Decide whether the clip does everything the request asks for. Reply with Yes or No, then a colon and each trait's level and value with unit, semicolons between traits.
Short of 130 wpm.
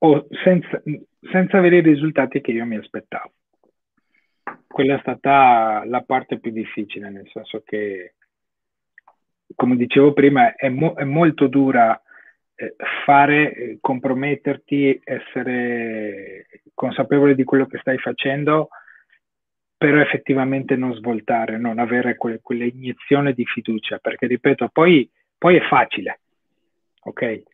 Yes: average, 120 wpm